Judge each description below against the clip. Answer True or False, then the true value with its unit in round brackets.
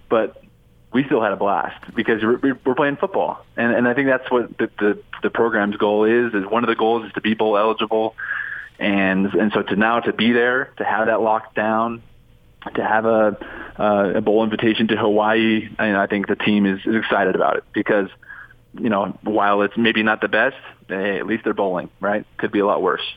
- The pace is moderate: False (220 wpm)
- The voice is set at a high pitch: False (110 Hz)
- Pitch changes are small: True (1.6 semitones)